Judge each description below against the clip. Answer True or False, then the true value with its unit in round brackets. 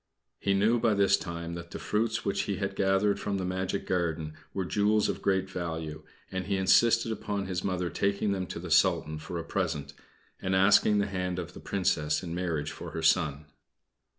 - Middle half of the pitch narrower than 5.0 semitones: True (2.8 semitones)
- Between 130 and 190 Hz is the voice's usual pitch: False (95 Hz)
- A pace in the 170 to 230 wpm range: True (200 wpm)